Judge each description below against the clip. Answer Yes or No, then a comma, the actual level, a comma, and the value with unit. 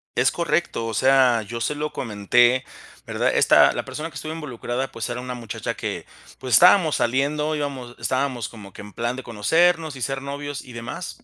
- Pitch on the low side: Yes, low, 130 Hz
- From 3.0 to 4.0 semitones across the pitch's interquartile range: Yes, average, 3.6 semitones